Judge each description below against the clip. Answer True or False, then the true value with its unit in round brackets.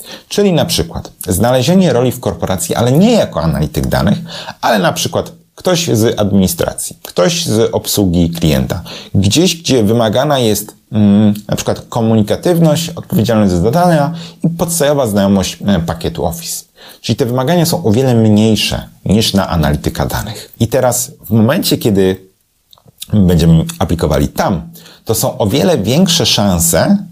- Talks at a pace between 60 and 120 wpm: False (140 wpm)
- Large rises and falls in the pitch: True (7.4 semitones)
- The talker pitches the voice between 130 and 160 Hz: False (110 Hz)